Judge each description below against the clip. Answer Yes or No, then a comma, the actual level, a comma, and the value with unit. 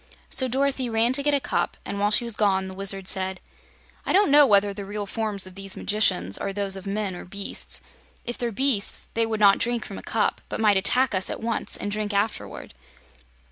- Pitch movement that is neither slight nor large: Yes, average, 3.1 semitones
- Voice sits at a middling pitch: No, high, 205 Hz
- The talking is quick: Yes, fast, 220 wpm